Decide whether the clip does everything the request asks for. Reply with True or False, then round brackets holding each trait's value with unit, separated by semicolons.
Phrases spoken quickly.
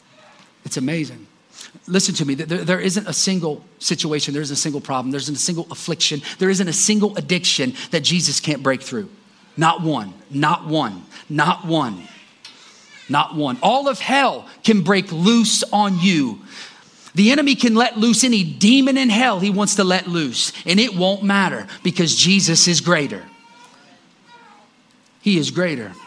False (165 wpm)